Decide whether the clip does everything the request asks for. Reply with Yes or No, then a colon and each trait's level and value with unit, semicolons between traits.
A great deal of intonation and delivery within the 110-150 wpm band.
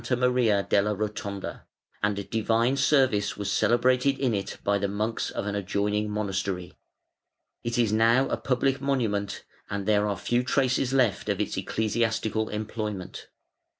No: average, 3.2 semitones; average, 145 wpm